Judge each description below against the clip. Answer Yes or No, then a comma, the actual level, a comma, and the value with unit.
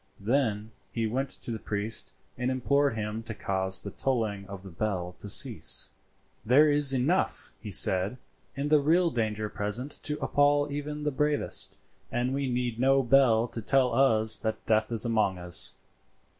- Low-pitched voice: Yes, low, 120 Hz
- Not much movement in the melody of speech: No, average, 4.5 semitones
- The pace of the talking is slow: No, average, 170 wpm